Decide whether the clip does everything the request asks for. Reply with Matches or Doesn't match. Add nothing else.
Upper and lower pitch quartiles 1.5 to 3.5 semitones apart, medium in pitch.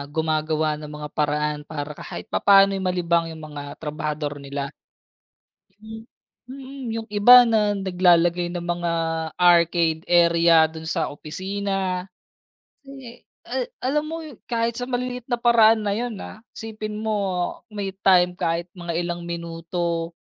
Doesn't match